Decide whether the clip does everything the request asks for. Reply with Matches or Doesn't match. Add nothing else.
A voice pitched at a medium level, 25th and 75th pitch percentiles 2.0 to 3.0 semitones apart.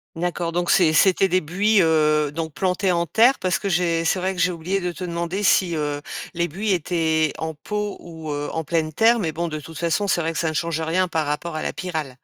Matches